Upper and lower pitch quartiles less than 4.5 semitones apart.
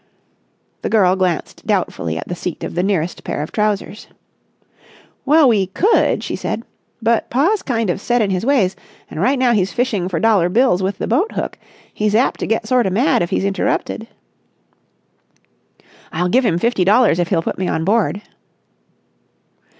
No: average, 4.9 semitones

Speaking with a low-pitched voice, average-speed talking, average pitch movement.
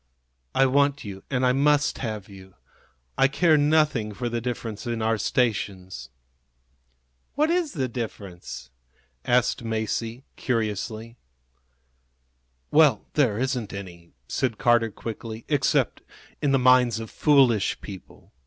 No: low, 120 Hz; slow, 125 wpm; average, 4.1 semitones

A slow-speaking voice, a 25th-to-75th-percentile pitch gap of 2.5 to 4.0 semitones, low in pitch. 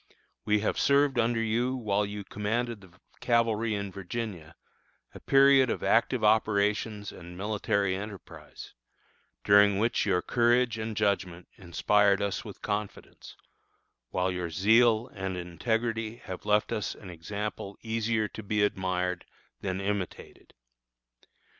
Yes: slow, 130 wpm; average, 2.8 semitones; low, 105 Hz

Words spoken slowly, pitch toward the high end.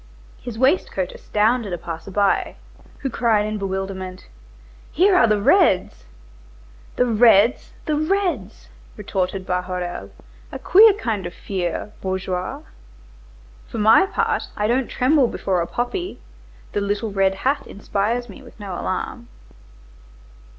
Yes: slow, 130 wpm; high, 210 Hz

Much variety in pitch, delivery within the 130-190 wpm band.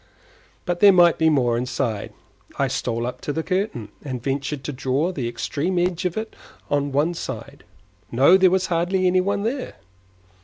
Yes: wide, 5.8 semitones; average, 180 wpm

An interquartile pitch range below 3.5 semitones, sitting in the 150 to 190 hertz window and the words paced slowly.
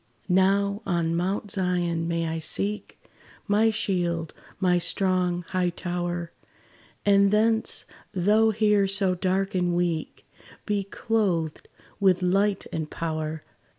Yes: average, 2.7 semitones; medium, 185 Hz; slow, 120 wpm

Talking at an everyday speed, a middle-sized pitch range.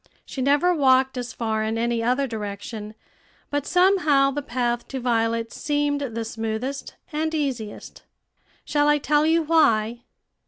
Yes: average, 150 wpm; average, 4.3 semitones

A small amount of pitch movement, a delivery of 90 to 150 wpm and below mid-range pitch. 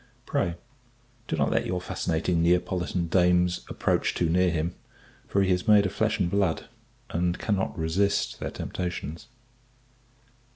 Yes: narrow, 2.0 semitones; average, 140 wpm; very low, 90 Hz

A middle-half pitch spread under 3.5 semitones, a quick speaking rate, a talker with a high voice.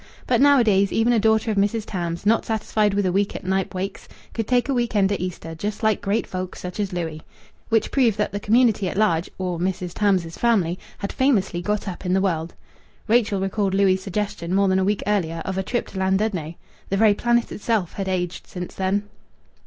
Yes: average, 2.8 semitones; fast, 215 wpm; high, 200 Hz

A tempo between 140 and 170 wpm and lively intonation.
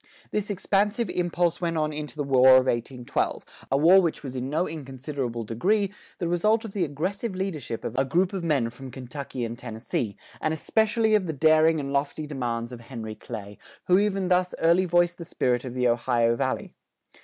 No: average, 190 wpm; wide, 6.2 semitones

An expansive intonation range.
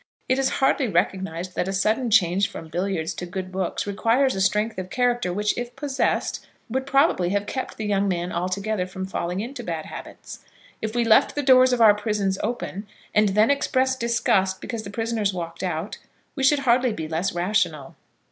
No: average, 4.7 semitones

